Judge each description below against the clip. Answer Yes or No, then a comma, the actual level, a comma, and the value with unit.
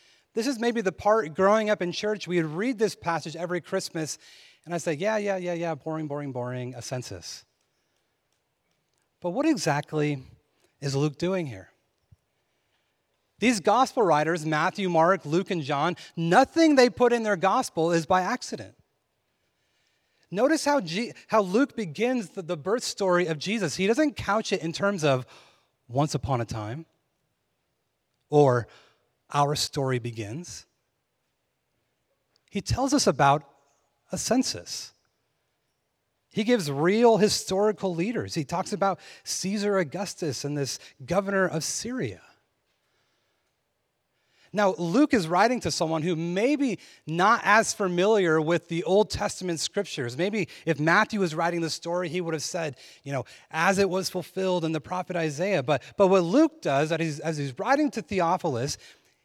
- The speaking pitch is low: No, medium, 175 Hz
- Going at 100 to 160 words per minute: Yes, average, 150 wpm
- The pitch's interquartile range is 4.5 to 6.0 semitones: Yes, average, 5.2 semitones